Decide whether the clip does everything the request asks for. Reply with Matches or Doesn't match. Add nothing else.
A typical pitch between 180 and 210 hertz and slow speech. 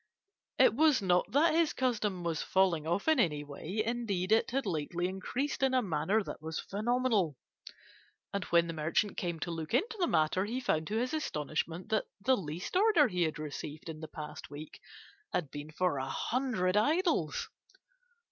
Doesn't match